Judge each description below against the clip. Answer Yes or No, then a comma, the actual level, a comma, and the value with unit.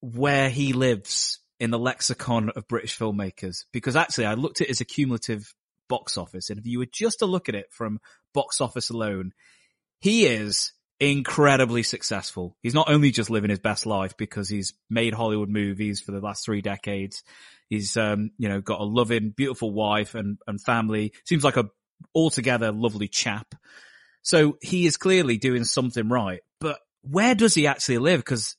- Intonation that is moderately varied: Yes, average, 4.6 semitones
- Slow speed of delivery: No, average, 180 wpm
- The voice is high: No, low, 115 Hz